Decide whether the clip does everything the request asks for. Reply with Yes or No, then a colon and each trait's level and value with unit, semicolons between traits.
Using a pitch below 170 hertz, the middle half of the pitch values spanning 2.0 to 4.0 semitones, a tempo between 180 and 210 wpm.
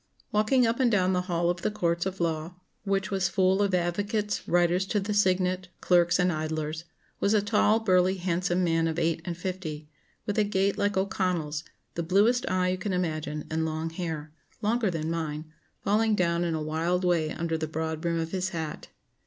No: medium, 180 Hz; average, 3.1 semitones; average, 200 wpm